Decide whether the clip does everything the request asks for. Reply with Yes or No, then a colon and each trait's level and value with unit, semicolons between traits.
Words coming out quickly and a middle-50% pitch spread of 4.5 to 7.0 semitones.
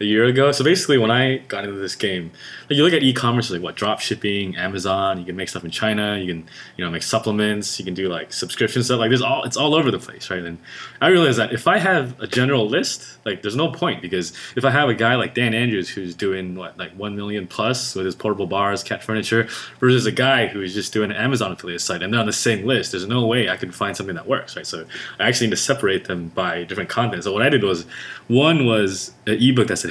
Yes: fast, 265 wpm; average, 4.8 semitones